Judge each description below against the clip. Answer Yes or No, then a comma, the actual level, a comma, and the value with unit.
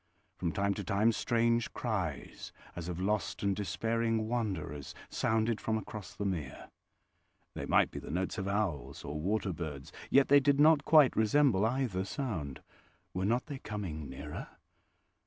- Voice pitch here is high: No, low, 105 Hz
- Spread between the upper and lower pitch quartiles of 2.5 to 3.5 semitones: No, average, 4.3 semitones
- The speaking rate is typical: Yes, average, 155 wpm